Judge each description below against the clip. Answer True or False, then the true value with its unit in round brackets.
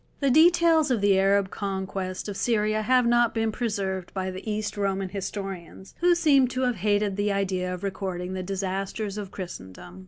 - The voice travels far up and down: False (3.1 semitones)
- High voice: True (200 Hz)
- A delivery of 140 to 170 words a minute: False (180 wpm)